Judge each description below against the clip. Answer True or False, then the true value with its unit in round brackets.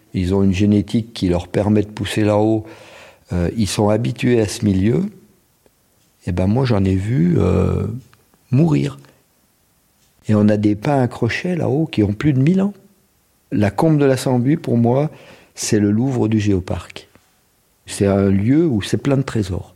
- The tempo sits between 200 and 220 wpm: False (175 wpm)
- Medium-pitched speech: False (110 Hz)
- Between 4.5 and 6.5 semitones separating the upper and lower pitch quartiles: True (5.1 semitones)